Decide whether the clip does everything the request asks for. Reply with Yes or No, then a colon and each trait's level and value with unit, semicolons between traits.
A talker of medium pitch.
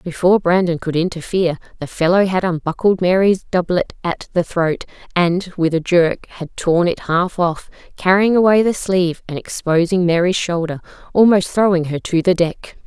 Yes: medium, 175 Hz